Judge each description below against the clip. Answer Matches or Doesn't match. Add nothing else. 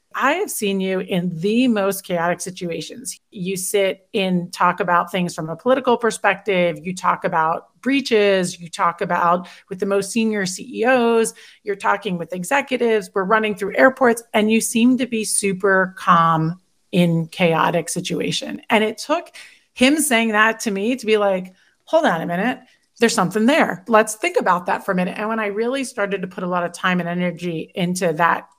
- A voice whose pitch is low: Doesn't match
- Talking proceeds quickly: Doesn't match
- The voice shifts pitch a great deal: Doesn't match